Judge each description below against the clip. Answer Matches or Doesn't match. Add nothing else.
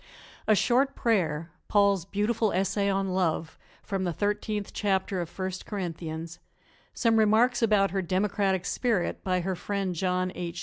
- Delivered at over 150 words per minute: Doesn't match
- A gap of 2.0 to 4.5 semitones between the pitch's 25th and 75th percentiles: Matches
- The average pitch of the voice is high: Matches